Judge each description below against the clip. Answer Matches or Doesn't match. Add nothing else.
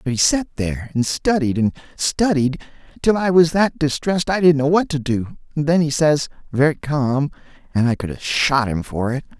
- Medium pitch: Matches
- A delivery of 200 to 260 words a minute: Matches